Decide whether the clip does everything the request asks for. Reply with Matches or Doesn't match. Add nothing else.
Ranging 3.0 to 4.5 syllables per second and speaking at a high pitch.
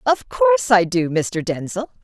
Doesn't match